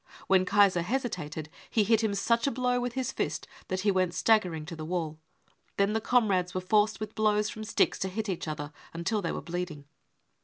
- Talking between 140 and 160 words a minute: No, fast, 205 wpm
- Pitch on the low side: No, high, 200 Hz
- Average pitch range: Yes, average, 3.8 semitones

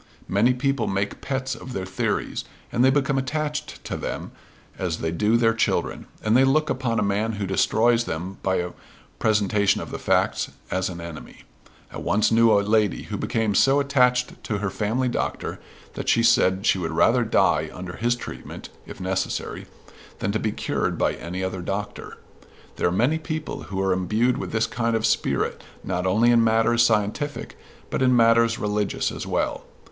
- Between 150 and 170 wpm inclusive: No, average, 185 wpm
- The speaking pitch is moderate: No, low, 110 Hz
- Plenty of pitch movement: No, average, 4.2 semitones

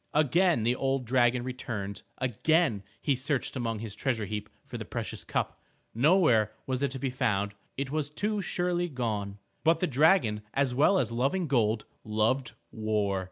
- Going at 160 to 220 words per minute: Yes, average, 165 wpm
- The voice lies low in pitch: Yes, low, 130 Hz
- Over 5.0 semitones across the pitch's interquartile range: Yes, wide, 5.4 semitones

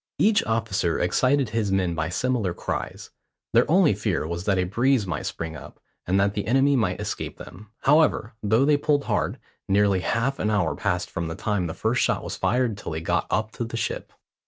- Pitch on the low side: Yes, low, 105 Hz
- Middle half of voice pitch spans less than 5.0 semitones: No, wide, 5.5 semitones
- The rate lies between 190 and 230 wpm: Yes, fast, 205 wpm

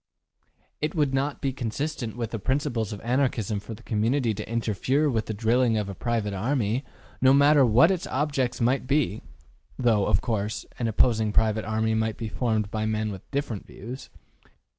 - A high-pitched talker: No, low, 115 Hz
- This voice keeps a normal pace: Yes, average, 180 wpm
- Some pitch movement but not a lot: Yes, average, 3.6 semitones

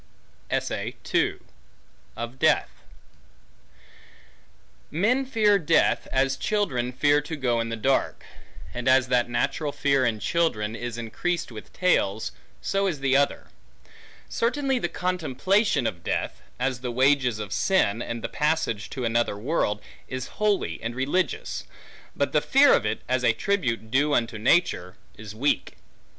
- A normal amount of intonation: No, wide, 6.4 semitones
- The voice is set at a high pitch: No, low, 130 Hz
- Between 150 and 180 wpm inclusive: No, slow, 135 wpm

